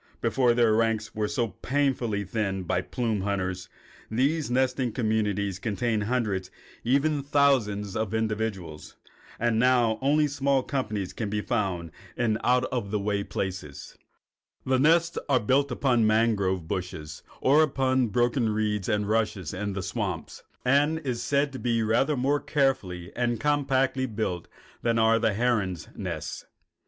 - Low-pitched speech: Yes, low, 115 Hz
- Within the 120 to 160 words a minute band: Yes, average, 155 wpm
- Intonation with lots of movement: No, average, 4.3 semitones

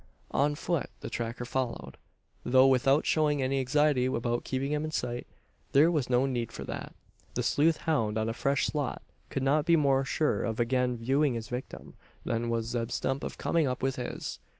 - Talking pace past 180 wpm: Yes, average, 195 wpm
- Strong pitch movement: No, average, 3.3 semitones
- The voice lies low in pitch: Yes, low, 130 Hz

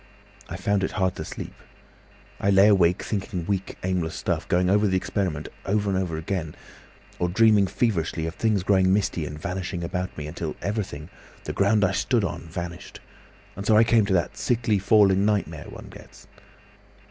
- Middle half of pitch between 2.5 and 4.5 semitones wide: Yes, average, 2.9 semitones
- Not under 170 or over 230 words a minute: Yes, average, 180 wpm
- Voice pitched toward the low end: Yes, very low, 95 Hz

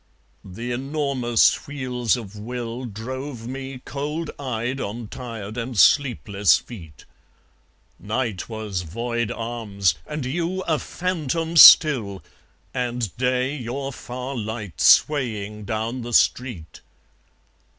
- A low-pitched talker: Yes, low, 120 Hz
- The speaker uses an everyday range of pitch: Yes, average, 3.6 semitones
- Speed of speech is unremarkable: No, slow, 110 wpm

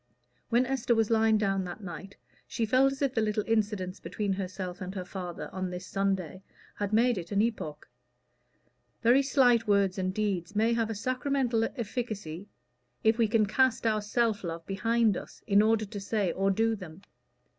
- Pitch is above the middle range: Yes, high, 210 Hz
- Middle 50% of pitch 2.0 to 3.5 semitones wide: Yes, average, 3.1 semitones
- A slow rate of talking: No, average, 180 wpm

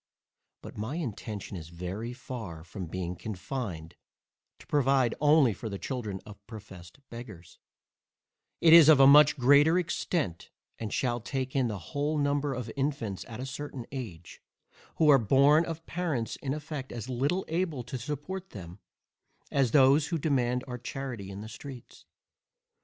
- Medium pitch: No, low, 130 Hz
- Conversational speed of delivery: Yes, average, 160 wpm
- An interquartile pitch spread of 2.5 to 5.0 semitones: No, wide, 5.4 semitones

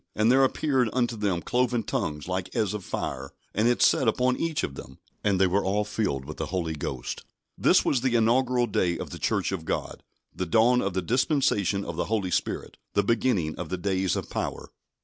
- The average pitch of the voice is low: Yes, low, 100 Hz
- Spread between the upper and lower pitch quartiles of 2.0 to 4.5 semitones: No, average, 5.2 semitones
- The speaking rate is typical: No, fast, 210 wpm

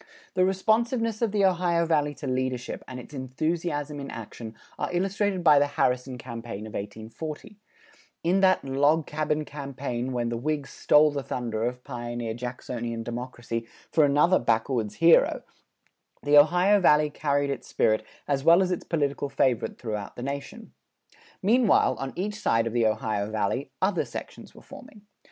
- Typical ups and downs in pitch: No, wide, 5.9 semitones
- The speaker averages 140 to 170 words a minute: Yes, average, 160 wpm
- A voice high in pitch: No, medium, 140 Hz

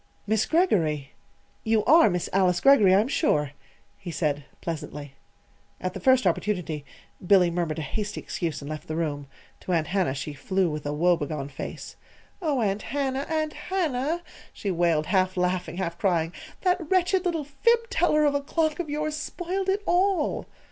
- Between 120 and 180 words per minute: Yes, average, 170 wpm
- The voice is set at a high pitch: Yes, high, 195 Hz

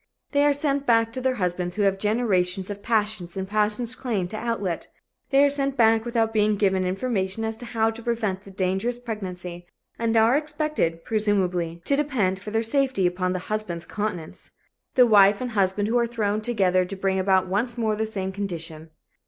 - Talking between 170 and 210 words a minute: Yes, average, 185 wpm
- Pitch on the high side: Yes, high, 210 Hz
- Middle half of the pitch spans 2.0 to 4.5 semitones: Yes, average, 3.8 semitones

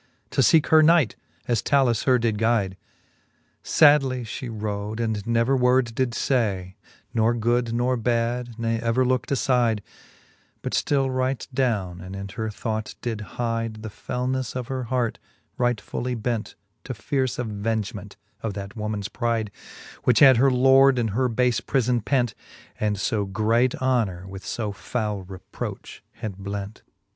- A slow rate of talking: No, average, 155 wpm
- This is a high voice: No, low, 115 Hz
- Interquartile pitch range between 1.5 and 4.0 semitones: Yes, average, 3.0 semitones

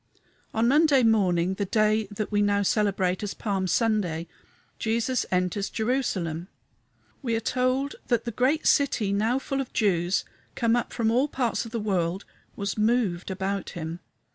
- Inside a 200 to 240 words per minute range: No, average, 160 wpm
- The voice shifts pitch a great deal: No, average, 3.9 semitones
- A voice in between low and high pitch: No, high, 215 Hz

